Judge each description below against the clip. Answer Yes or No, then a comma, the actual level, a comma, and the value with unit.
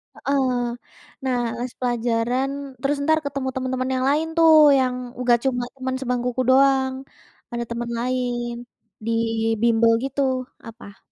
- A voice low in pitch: No, very high, 255 Hz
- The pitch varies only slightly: Yes, narrow, 1.9 semitones